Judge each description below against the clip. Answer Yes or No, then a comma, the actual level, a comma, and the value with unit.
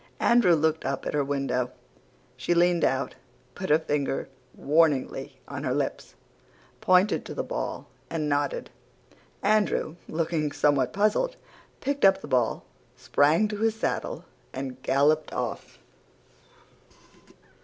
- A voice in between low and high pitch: Yes, medium, 155 Hz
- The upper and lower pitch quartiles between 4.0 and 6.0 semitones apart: Yes, average, 5.0 semitones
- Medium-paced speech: No, slow, 125 wpm